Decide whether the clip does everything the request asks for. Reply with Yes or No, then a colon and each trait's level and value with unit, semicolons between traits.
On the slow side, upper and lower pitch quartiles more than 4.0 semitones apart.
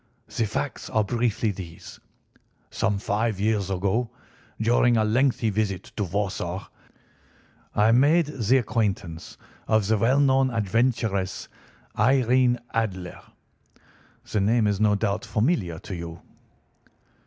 No: slow, 120 wpm; average, 3.5 semitones